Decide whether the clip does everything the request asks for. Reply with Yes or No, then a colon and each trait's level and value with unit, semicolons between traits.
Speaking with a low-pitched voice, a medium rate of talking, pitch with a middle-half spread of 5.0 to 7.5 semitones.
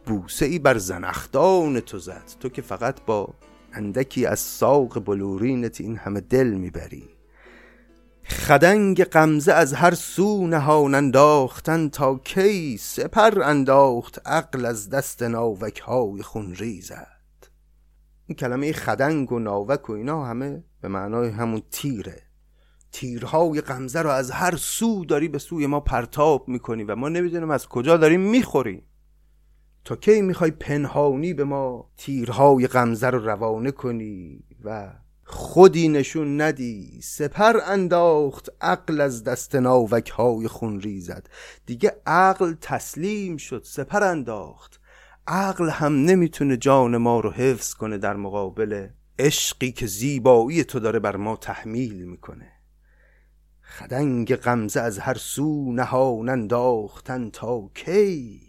Yes: low, 130 Hz; average, 130 wpm; wide, 5.5 semitones